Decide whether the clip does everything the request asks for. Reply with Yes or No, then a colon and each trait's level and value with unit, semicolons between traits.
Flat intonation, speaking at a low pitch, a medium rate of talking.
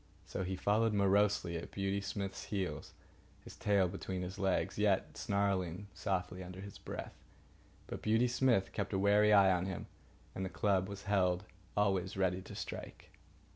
Yes: narrow, 1.6 semitones; very low, 95 Hz; average, 165 wpm